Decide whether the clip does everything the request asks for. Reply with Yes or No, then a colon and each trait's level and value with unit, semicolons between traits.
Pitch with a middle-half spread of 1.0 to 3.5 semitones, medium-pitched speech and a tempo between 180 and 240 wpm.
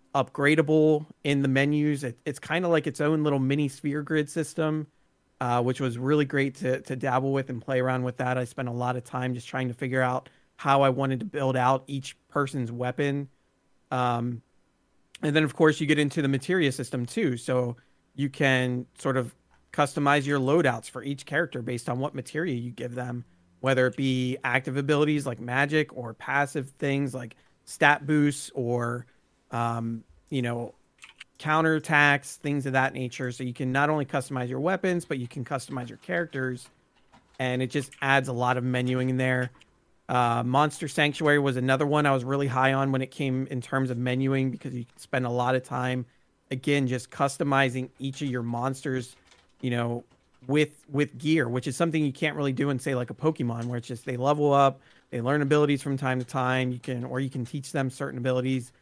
No: narrow, 2.4 semitones; low, 130 Hz; average, 200 wpm